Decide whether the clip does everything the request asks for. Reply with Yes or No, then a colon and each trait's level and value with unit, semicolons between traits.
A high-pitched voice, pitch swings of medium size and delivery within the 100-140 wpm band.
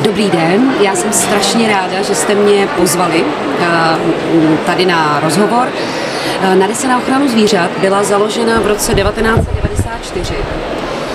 Yes: high, 200 Hz; average, 3.2 semitones; average, 120 wpm